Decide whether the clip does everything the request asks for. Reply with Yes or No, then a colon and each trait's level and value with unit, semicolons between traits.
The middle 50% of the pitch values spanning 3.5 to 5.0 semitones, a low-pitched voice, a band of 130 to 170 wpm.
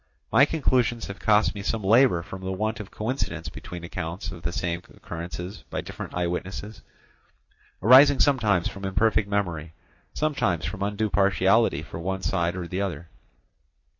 Yes: average, 3.9 semitones; very low, 95 Hz; average, 160 wpm